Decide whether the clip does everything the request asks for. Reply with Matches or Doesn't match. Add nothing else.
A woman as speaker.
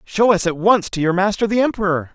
Doesn't match